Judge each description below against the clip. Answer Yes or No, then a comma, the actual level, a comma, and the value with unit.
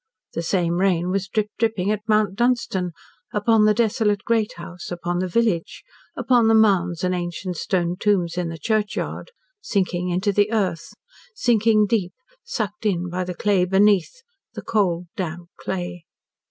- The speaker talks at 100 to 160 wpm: Yes, average, 155 wpm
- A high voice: Yes, high, 195 Hz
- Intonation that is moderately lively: Yes, average, 3.3 semitones